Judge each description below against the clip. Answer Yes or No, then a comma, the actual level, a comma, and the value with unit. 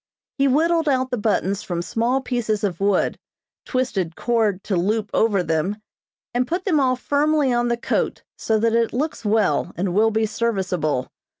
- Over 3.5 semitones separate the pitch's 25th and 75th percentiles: Yes, average, 4.4 semitones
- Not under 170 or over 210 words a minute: Yes, average, 175 wpm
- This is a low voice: No, high, 225 Hz